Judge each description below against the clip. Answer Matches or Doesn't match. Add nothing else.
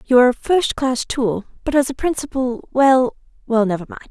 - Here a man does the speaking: Doesn't match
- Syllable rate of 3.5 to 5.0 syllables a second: Doesn't match